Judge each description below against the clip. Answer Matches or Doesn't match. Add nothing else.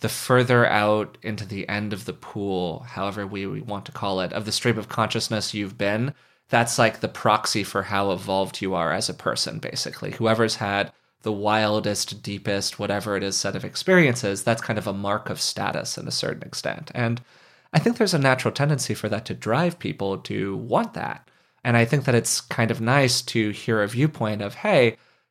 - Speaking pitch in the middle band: Doesn't match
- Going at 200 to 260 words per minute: Matches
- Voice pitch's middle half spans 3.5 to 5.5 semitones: Doesn't match